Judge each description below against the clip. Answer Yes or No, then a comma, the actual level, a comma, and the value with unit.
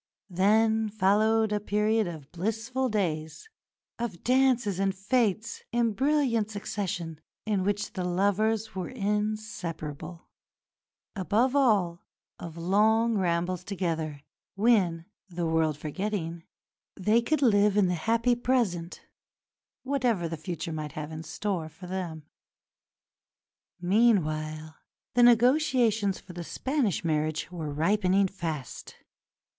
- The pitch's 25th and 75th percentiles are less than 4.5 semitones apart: No, average, 4.8 semitones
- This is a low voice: No, high, 195 Hz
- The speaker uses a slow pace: Yes, slow, 115 wpm